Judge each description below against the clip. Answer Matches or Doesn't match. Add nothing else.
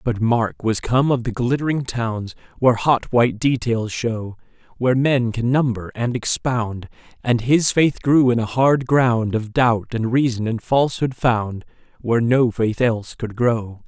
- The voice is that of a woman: Doesn't match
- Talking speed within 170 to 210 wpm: Matches